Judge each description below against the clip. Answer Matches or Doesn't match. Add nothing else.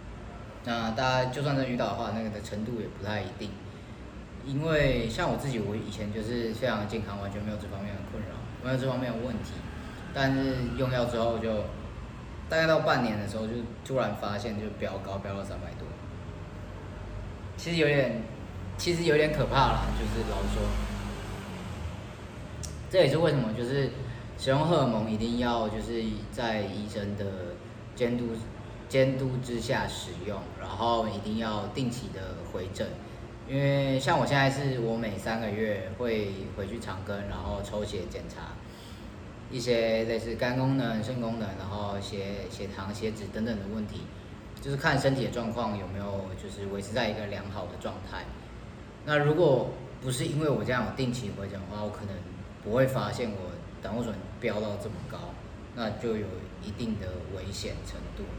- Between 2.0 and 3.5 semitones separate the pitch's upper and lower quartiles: Matches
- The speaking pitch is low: Matches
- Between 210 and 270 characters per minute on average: Matches